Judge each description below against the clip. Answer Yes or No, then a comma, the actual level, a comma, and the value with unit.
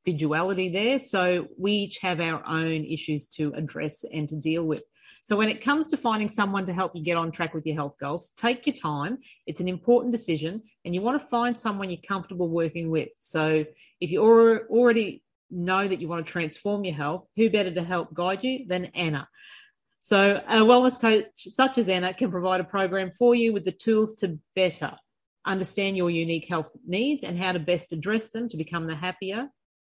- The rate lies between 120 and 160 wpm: No, fast, 205 wpm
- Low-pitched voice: No, medium, 185 Hz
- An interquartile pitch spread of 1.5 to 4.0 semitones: No, average, 5.2 semitones